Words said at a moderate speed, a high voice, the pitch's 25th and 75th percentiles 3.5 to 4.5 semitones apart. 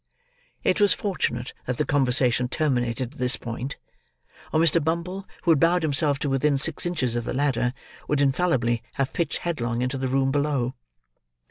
No: average, 170 wpm; low, 135 Hz; average, 4.2 semitones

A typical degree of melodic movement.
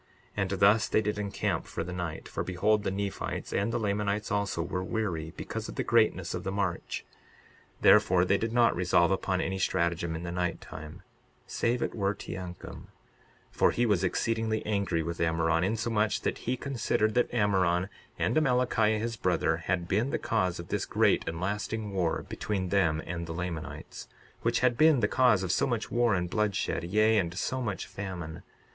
Yes: average, 3.8 semitones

